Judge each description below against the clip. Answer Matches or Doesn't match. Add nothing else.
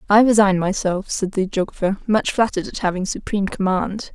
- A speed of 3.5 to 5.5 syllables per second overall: Doesn't match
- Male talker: Doesn't match